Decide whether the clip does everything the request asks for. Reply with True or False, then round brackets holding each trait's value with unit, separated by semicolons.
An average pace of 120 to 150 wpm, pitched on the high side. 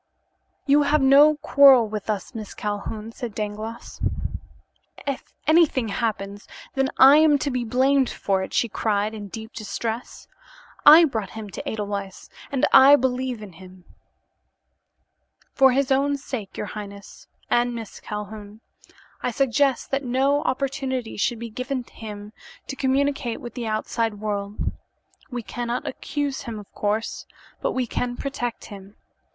True (145 wpm; 235 Hz)